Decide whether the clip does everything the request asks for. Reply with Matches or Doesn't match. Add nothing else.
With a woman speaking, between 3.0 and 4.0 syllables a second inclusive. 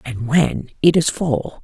Matches